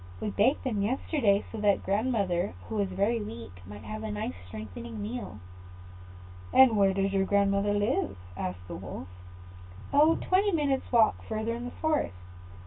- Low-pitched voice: No, high, 200 Hz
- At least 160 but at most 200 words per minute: Yes, average, 170 wpm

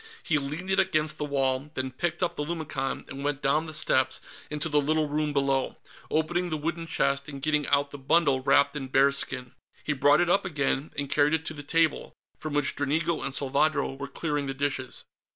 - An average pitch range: No, narrow, 2.2 semitones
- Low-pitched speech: No, medium, 145 Hz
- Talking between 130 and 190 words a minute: No, fast, 205 wpm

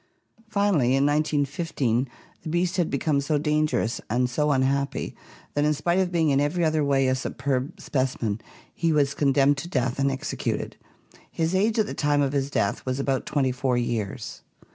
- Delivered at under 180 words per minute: No, average, 185 wpm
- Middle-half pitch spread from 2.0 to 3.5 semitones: Yes, average, 2.9 semitones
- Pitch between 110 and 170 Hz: Yes, medium, 140 Hz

